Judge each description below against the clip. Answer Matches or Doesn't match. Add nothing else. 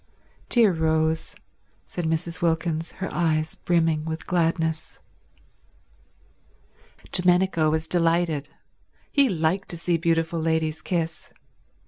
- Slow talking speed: Matches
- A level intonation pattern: Matches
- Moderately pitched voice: Matches